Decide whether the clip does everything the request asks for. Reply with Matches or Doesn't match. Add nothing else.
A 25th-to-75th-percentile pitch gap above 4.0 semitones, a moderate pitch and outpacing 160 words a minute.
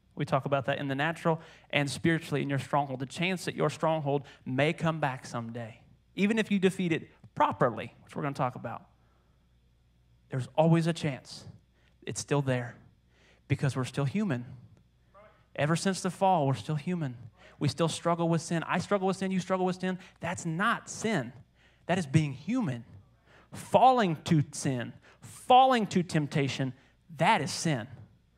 Matches